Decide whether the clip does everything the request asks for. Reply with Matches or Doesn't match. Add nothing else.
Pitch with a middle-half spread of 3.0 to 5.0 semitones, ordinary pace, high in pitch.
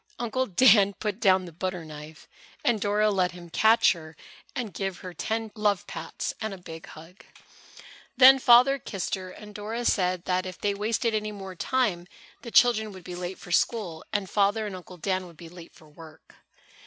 Matches